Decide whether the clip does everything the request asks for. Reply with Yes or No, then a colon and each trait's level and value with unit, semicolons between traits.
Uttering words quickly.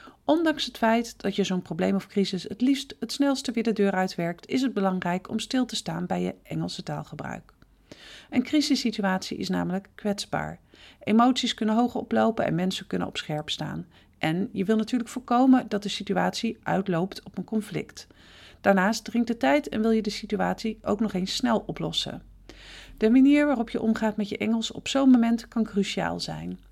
No: average, 185 wpm